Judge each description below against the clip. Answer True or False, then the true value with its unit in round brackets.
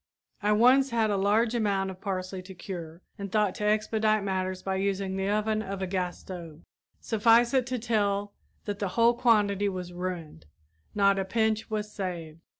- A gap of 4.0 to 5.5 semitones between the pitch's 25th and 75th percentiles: False (2.5 semitones)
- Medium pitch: False (200 Hz)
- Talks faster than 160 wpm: True (180 wpm)